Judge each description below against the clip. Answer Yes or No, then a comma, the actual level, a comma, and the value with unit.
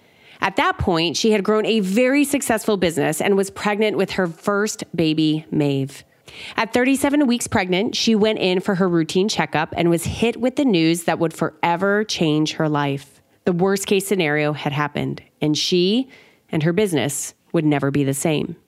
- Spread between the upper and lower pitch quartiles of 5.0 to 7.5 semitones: Yes, wide, 5.5 semitones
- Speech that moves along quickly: No, average, 185 wpm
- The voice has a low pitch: No, medium, 185 Hz